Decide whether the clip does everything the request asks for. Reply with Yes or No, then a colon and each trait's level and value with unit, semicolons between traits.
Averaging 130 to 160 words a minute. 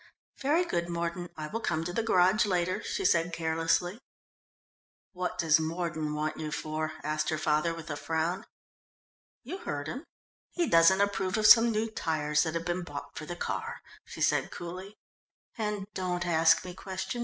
No: average, 175 wpm